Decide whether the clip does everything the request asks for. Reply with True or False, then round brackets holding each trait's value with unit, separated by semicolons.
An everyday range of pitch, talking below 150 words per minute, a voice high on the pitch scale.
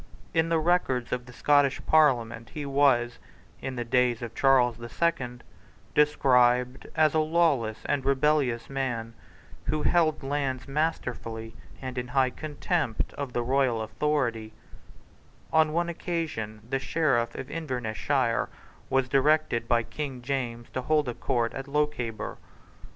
False (3.8 semitones; 140 wpm; 130 Hz)